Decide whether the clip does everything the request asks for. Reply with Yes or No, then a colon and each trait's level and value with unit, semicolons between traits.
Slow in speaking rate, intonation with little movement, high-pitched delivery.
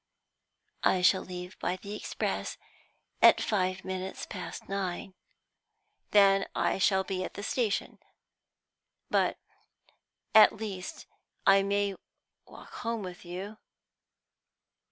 Yes: slow, 110 wpm; narrow, 1.6 semitones; high, 195 Hz